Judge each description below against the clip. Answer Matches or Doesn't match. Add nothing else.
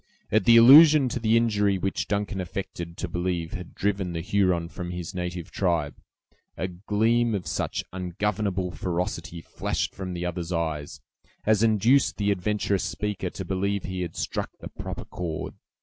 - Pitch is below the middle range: Matches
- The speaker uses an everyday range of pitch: Matches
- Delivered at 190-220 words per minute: Doesn't match